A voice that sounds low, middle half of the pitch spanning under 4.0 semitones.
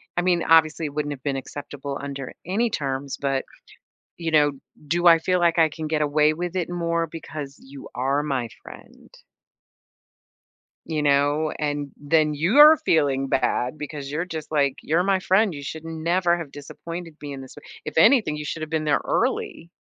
No: medium, 155 Hz; average, 2.8 semitones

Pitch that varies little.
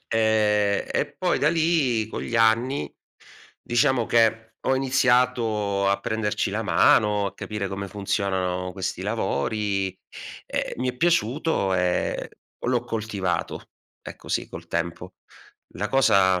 No: average, 3.5 semitones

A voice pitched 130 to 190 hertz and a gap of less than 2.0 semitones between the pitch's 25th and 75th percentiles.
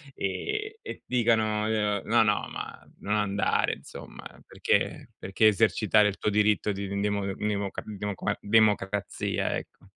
No: low, 105 Hz; narrow, 1.4 semitones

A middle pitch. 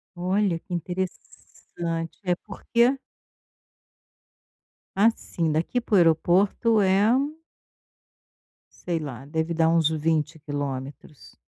Yes: medium, 170 Hz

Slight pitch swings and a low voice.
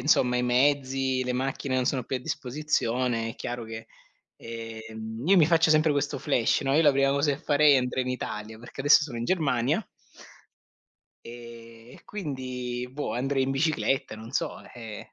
No: average, 3.3 semitones; low, 130 Hz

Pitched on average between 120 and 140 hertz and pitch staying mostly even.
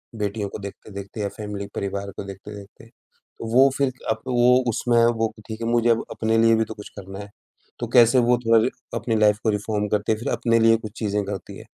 No: low, 110 Hz; narrow, 2.0 semitones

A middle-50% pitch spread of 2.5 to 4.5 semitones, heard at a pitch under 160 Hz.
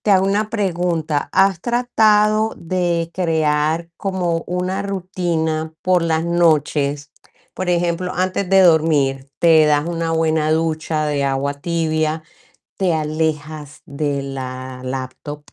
No: average, 3.2 semitones; medium, 165 Hz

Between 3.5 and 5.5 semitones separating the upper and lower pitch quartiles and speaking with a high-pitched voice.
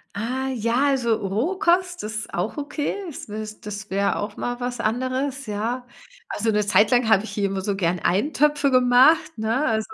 Yes: average, 4.2 semitones; high, 230 Hz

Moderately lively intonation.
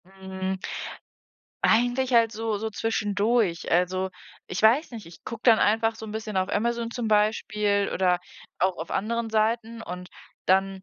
Yes: average, 3.1 semitones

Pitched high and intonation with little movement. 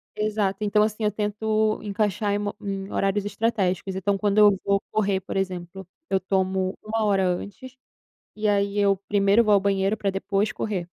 Yes: high, 200 Hz; narrow, 1.6 semitones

